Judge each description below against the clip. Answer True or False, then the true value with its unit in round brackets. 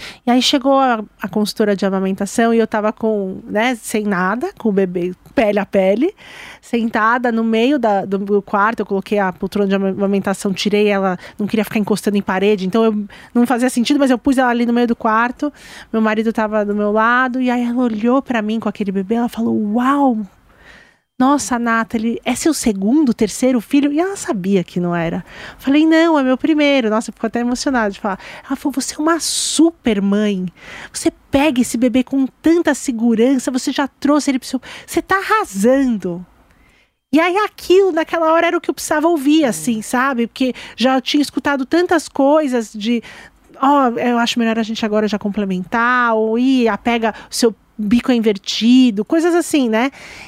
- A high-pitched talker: True (235 Hz)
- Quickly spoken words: True (190 wpm)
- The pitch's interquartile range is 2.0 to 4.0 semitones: False (4.5 semitones)